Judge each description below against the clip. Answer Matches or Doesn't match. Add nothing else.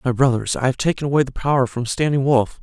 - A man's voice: Matches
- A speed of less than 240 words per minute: Doesn't match